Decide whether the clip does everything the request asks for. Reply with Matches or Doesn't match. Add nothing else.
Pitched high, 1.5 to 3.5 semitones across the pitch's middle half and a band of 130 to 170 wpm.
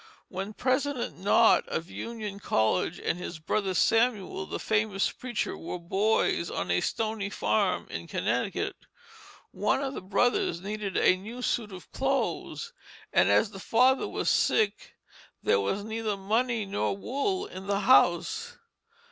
Doesn't match